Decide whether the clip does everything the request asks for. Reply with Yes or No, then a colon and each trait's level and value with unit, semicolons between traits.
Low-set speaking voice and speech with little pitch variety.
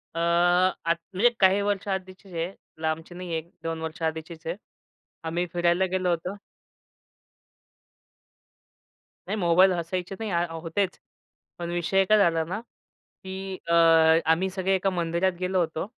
No: medium, 175 Hz; narrow, 2.2 semitones